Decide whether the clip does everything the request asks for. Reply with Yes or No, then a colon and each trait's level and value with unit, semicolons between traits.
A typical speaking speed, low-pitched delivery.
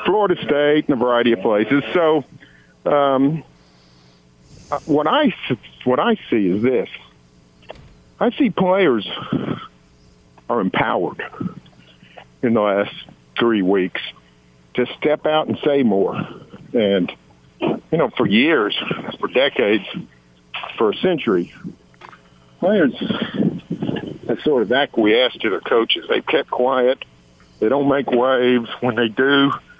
No: slow, 120 wpm; low, 120 Hz